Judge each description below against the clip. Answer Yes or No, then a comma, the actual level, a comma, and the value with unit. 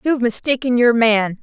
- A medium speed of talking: Yes, average, 170 wpm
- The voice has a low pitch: No, high, 235 Hz